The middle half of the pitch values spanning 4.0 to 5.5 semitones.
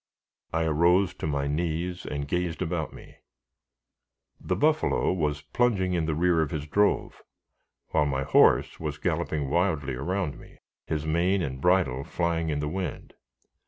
No: average, 3.5 semitones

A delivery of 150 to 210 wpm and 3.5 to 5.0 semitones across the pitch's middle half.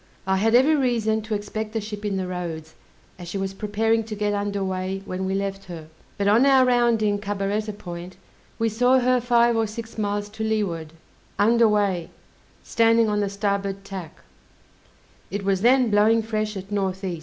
No: average, 185 wpm; narrow, 2.5 semitones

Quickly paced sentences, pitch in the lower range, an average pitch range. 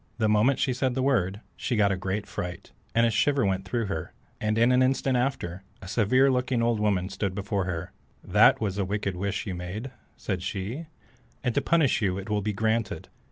Yes: fast, 210 wpm; low, 105 Hz; average, 4.3 semitones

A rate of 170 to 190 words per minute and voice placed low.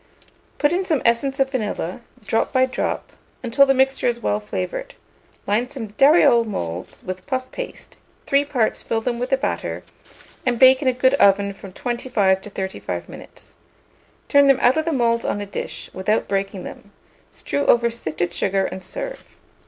No: average, 175 wpm; high, 235 Hz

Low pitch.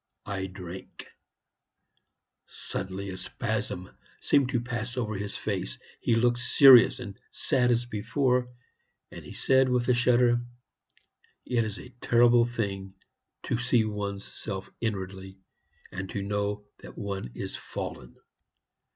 Yes: low, 110 Hz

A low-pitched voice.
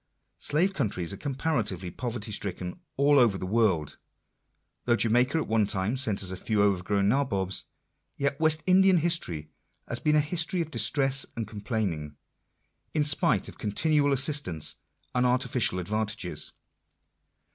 Yes: low, 115 Hz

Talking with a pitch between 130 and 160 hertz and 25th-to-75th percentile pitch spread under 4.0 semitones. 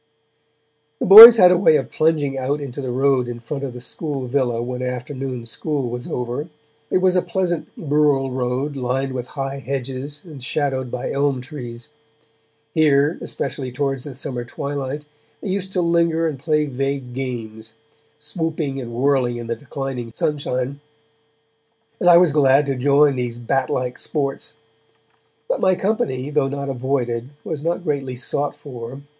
Yes: low, 135 Hz; average, 2.9 semitones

